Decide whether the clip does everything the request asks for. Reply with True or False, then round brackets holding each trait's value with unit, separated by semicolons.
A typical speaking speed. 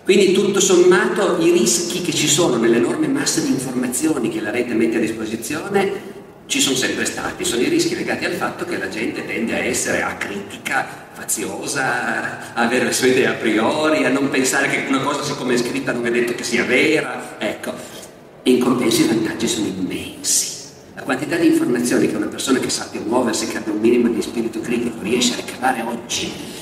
False (195 wpm)